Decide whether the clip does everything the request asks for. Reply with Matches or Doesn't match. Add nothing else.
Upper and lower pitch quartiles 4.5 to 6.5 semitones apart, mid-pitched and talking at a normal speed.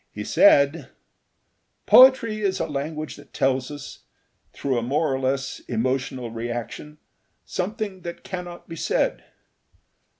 Doesn't match